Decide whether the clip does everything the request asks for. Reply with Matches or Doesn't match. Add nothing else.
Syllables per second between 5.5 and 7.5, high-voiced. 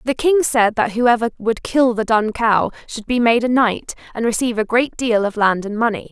Doesn't match